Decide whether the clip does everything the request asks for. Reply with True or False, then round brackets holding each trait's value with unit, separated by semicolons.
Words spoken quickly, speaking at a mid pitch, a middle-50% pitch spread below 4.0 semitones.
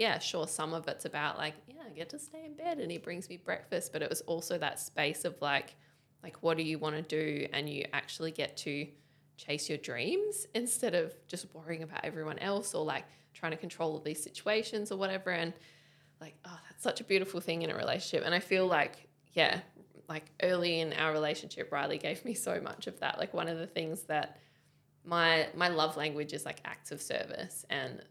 True (220 wpm; 165 Hz; 2.9 semitones)